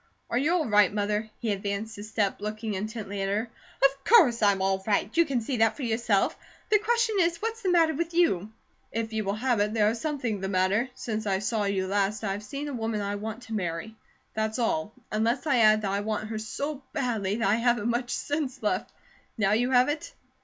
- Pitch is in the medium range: No, high, 220 Hz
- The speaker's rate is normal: No, fast, 225 wpm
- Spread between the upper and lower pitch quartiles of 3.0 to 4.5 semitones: Yes, average, 4.1 semitones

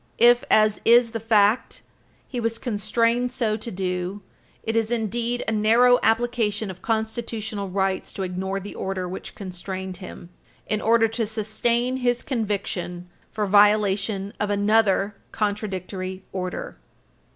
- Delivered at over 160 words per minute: No, slow, 135 wpm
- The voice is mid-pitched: No, high, 210 Hz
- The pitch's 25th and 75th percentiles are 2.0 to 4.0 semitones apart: Yes, average, 2.9 semitones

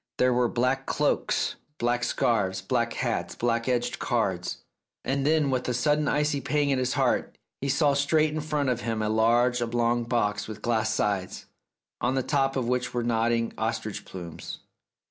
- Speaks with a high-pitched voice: No, low, 120 Hz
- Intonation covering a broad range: No, average, 2.9 semitones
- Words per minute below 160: No, average, 175 wpm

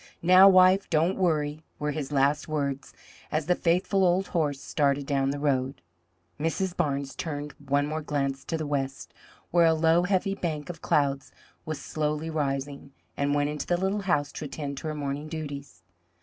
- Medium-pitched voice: Yes, medium, 150 Hz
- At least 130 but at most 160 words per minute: No, average, 175 wpm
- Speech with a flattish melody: No, average, 3.1 semitones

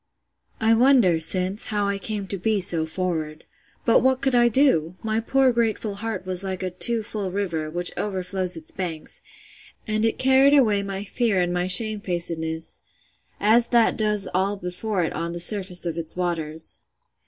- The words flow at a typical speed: Yes, average, 170 wpm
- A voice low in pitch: No, high, 195 Hz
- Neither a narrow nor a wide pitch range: Yes, average, 4.0 semitones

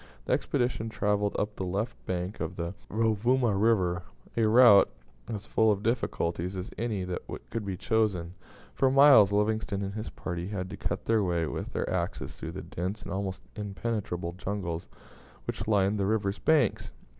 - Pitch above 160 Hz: No, low, 100 Hz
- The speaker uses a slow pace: No, average, 170 wpm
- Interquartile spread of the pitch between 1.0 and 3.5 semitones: Yes, average, 3.2 semitones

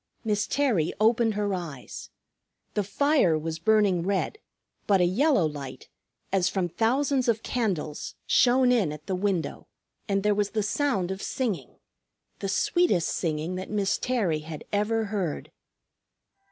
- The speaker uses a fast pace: No, average, 145 wpm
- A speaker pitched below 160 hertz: No, high, 200 Hz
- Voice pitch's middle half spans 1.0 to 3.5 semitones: No, average, 4.5 semitones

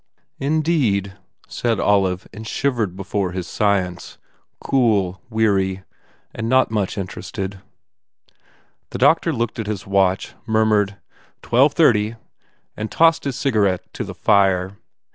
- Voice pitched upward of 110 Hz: No, low, 105 Hz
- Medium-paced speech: No, slow, 115 wpm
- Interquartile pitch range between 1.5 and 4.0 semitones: Yes, average, 3.2 semitones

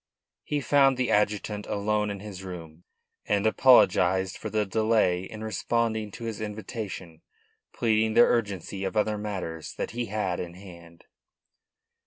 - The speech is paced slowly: No, average, 145 wpm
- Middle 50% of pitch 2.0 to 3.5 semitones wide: Yes, average, 2.8 semitones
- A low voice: Yes, low, 105 Hz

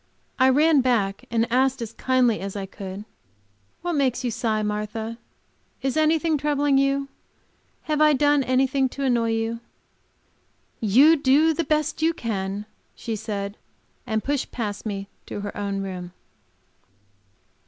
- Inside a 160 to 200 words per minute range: No, average, 145 wpm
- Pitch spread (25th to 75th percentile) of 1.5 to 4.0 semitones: No, average, 5.1 semitones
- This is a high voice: Yes, high, 245 Hz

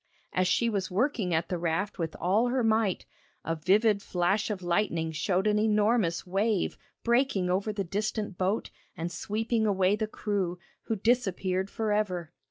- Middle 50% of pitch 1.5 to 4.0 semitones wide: Yes, average, 3.2 semitones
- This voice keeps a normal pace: Yes, average, 165 wpm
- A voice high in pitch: Yes, high, 200 Hz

